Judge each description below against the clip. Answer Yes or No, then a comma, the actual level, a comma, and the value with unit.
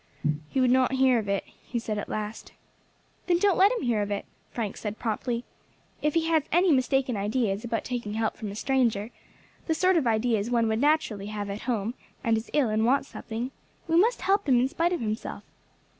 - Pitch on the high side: Yes, high, 240 Hz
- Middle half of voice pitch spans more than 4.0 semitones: Yes, average, 4.4 semitones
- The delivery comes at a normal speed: No, fast, 210 wpm